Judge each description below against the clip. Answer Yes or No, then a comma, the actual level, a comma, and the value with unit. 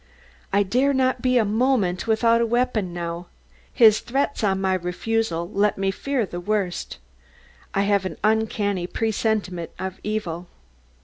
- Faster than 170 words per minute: No, average, 145 wpm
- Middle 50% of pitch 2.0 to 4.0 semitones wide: Yes, average, 3.6 semitones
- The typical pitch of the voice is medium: No, high, 210 Hz